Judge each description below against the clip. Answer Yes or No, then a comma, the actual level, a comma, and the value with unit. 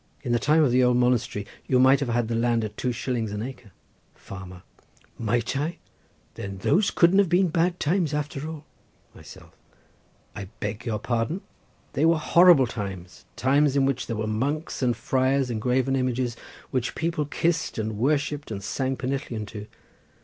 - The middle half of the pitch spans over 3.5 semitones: Yes, average, 4.5 semitones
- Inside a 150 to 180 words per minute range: Yes, average, 170 wpm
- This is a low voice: Yes, low, 130 Hz